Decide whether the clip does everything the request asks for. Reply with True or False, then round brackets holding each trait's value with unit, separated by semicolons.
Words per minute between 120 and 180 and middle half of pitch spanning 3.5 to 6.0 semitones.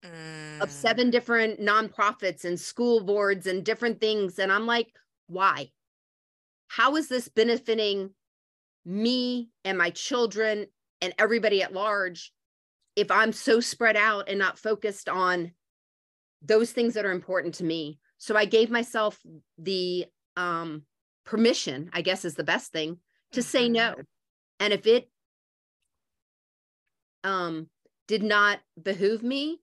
True (135 wpm; 4.6 semitones)